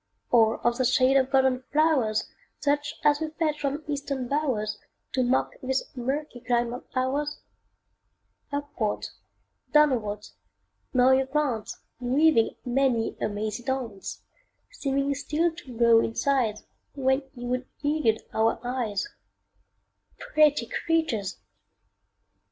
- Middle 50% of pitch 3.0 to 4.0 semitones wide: Yes, average, 3.5 semitones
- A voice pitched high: Yes, very high, 260 Hz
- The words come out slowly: Yes, slow, 120 wpm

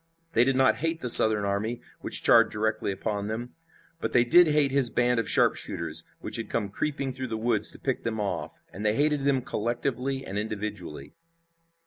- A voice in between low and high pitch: No, low, 115 Hz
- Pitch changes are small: No, average, 3.9 semitones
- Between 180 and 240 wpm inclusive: Yes, average, 190 wpm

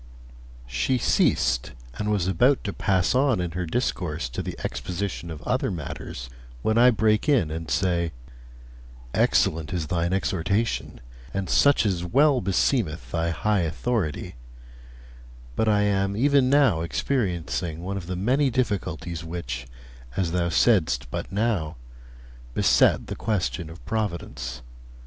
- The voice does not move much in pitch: No, average, 5.0 semitones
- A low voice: Yes, very low, 90 Hz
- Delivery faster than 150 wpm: No, average, 140 wpm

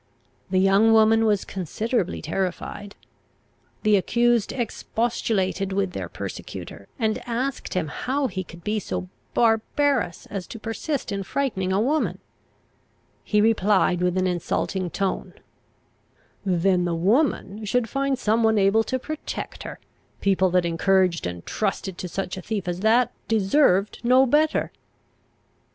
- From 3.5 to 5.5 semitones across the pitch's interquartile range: Yes, average, 3.9 semitones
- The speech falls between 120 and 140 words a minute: Yes, slow, 135 wpm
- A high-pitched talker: Yes, high, 205 Hz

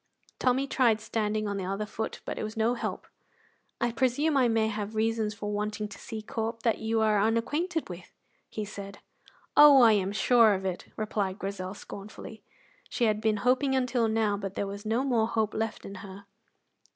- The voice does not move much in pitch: Yes, narrow, 2.2 semitones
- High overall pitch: Yes, high, 220 Hz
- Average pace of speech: Yes, average, 190 wpm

